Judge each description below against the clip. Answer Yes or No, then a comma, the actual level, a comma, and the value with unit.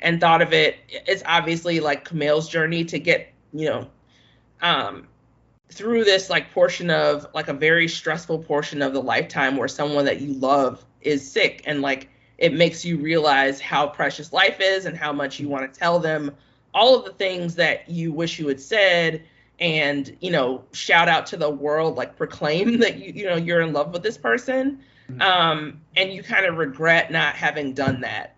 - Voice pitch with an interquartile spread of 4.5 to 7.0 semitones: No, average, 3.2 semitones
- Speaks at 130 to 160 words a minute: No, average, 195 wpm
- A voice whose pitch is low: No, medium, 160 Hz